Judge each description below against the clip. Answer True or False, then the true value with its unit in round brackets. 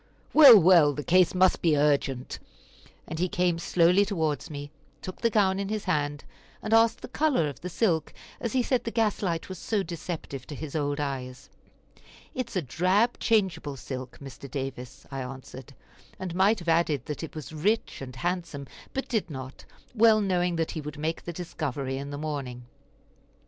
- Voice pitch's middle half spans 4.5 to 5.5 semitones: True (5.1 semitones)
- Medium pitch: True (165 Hz)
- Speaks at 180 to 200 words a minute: True (185 wpm)